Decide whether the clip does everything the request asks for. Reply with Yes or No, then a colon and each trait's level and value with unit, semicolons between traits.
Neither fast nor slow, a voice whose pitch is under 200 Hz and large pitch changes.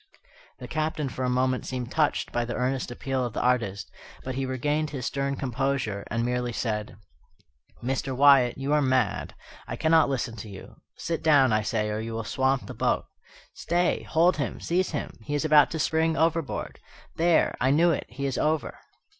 No: average, 190 wpm; low, 135 Hz; average, 3.8 semitones